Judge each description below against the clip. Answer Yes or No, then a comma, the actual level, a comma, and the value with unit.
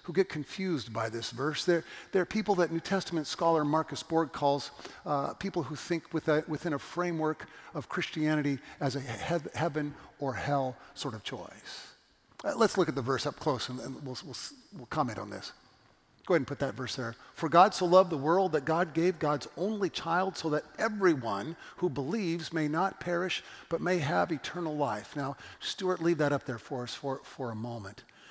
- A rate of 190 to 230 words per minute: Yes, average, 200 wpm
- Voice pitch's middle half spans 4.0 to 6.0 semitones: Yes, average, 4.3 semitones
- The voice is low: No, medium, 155 Hz